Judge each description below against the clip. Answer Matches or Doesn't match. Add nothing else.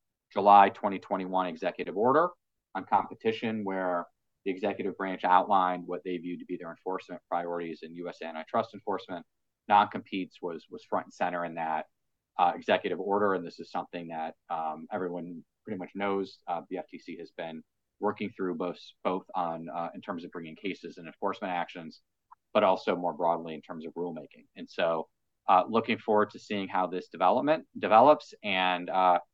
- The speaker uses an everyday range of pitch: Doesn't match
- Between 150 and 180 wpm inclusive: Matches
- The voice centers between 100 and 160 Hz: Doesn't match